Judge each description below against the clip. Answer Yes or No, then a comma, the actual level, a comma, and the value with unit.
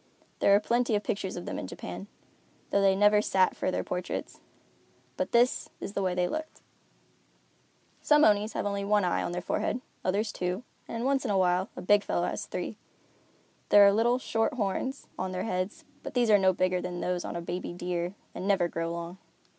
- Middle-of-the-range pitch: No, high, 195 Hz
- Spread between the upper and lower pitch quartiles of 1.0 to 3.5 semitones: Yes, average, 2.8 semitones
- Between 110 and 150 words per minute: No, fast, 205 wpm